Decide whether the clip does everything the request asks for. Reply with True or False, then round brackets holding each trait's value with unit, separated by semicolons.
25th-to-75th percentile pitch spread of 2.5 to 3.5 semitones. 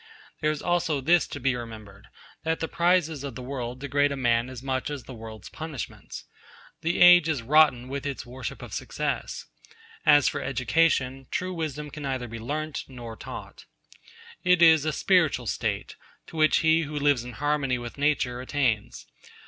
False (3.9 semitones)